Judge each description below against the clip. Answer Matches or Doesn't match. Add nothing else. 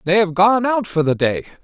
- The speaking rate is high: Matches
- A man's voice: Matches